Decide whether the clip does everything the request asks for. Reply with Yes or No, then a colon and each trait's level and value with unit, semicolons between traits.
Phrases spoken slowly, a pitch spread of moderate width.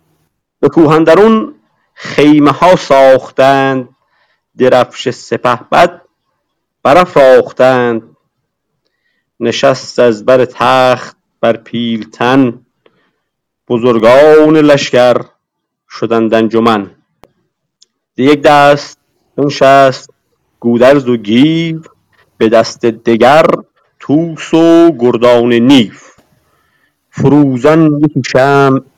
Yes: slow, 70 wpm; average, 3.6 semitones